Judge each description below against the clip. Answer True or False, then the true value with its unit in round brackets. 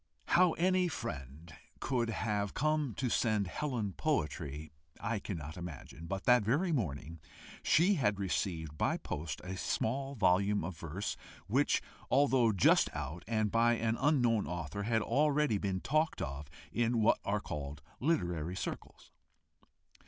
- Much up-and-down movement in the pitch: True (7.2 semitones)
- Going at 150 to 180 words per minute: False (140 wpm)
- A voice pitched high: False (105 Hz)